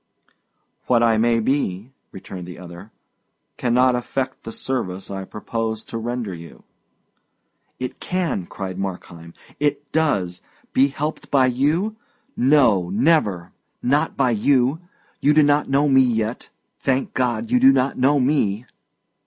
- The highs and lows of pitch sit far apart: Yes, wide, 6.2 semitones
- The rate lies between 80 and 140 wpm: Yes, slow, 135 wpm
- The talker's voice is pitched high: No, low, 125 Hz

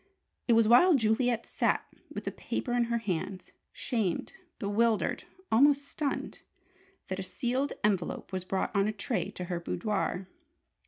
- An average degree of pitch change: Yes, average, 4.0 semitones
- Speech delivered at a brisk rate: No, average, 150 wpm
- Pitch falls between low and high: No, high, 220 Hz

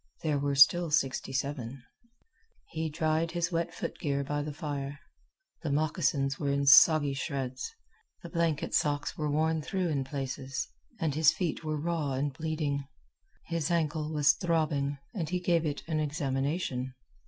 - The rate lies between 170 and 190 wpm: No, average, 155 wpm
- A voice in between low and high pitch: Yes, medium, 150 Hz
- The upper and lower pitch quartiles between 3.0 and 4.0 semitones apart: No, narrow, 2.5 semitones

